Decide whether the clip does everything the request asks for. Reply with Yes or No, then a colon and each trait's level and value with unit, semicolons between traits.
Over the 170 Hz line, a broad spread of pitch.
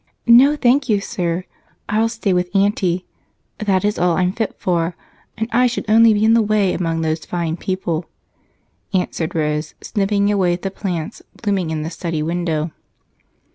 No: medium, 185 Hz; average, 4.1 semitones